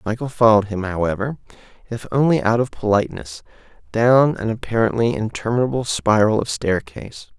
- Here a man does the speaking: Yes, male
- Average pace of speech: No, slow, 130 wpm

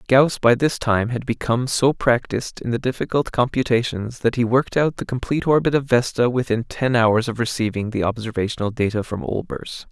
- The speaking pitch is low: Yes, low, 120 Hz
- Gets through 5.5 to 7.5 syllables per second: Yes, 5.6 syllables/s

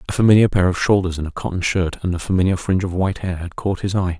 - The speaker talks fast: Yes, fast, 285 wpm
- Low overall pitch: Yes, very low, 90 Hz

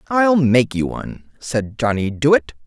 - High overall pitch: No, low, 130 Hz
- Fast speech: No, average, 160 wpm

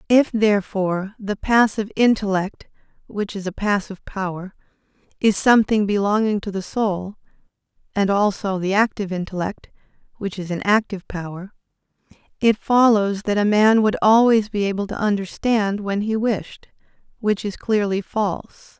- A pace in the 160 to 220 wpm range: No, average, 140 wpm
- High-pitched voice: Yes, high, 205 Hz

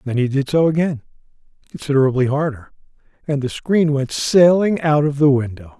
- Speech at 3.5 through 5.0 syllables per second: No, 5.4 syllables/s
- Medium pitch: Yes, medium, 145 Hz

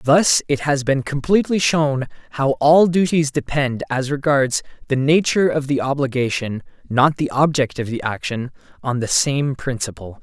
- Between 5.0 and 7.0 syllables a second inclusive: No, 4.5 syllables/s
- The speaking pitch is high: No, medium, 140 Hz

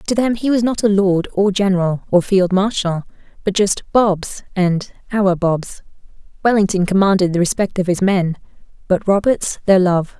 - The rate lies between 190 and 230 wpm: No, average, 170 wpm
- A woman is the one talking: Yes, female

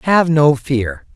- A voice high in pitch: No, medium, 140 Hz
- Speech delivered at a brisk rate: No, average, 155 wpm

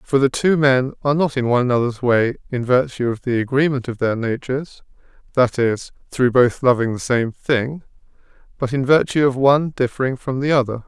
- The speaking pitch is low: Yes, low, 130 Hz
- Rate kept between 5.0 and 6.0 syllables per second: Yes, 5.5 syllables/s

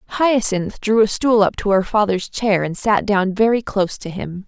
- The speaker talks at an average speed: No, fast, 215 wpm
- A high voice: Yes, high, 205 Hz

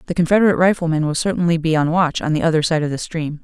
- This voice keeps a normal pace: No, fast, 260 wpm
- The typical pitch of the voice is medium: Yes, medium, 165 Hz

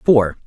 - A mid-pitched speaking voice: No, low, 120 Hz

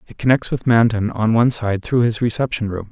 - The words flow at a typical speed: No, fast, 225 wpm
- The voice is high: No, low, 115 Hz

